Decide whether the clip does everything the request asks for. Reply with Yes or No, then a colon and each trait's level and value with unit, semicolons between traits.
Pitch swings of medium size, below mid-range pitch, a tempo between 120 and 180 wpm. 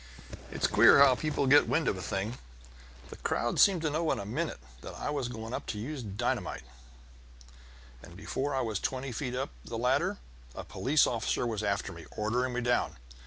No: average, 4.4 semitones; low, 125 Hz; average, 190 wpm